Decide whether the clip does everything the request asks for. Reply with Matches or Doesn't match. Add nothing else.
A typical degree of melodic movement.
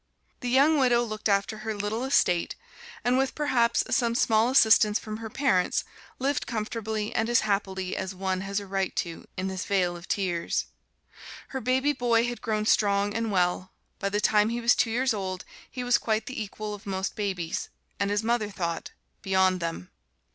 Matches